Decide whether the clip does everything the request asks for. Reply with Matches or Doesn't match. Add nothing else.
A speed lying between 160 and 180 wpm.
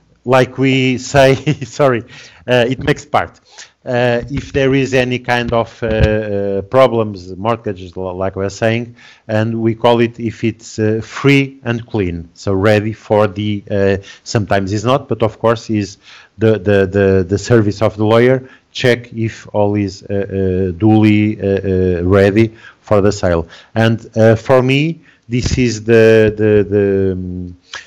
Matches